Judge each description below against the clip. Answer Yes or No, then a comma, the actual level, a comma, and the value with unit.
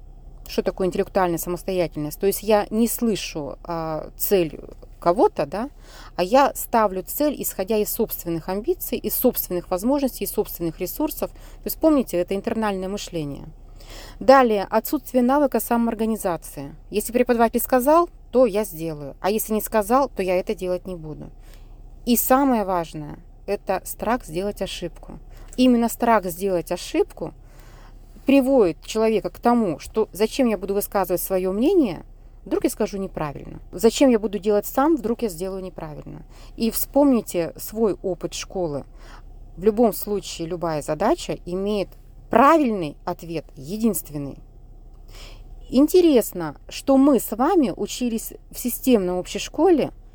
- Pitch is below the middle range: No, high, 200 Hz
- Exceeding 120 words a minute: Yes, average, 135 wpm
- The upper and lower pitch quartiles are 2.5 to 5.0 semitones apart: No, wide, 5.6 semitones